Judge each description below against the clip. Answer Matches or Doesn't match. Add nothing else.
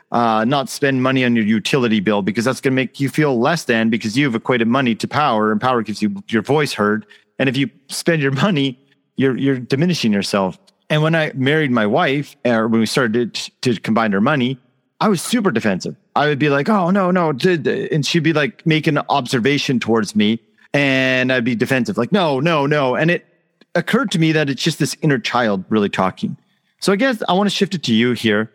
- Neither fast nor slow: Doesn't match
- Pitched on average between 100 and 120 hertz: Doesn't match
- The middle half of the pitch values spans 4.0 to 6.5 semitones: Matches